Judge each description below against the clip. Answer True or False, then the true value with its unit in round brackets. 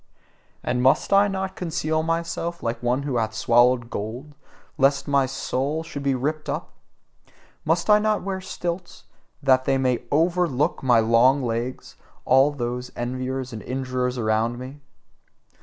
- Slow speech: False (145 wpm)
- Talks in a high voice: False (135 Hz)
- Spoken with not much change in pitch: False (4.5 semitones)